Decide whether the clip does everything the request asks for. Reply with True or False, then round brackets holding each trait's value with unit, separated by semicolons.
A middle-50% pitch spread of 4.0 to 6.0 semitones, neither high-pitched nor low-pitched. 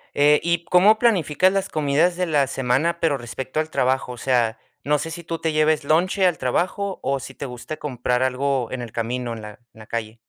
True (5.1 semitones; 145 Hz)